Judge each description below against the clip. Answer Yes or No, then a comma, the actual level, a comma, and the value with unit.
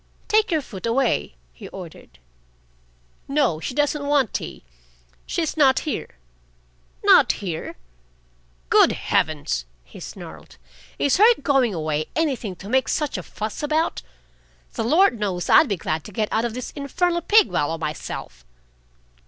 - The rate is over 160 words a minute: No, average, 145 wpm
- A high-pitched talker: Yes, very high, 250 Hz